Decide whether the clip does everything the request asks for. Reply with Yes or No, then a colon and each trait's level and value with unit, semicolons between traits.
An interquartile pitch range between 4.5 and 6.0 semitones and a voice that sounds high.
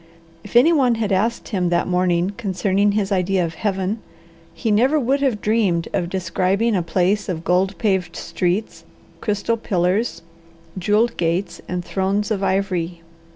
No: average, 3.1 semitones; high, 195 Hz